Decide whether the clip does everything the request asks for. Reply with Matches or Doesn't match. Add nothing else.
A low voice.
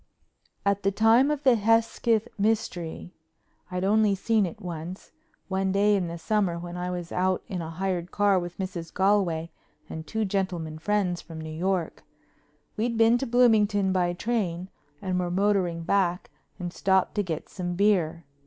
Doesn't match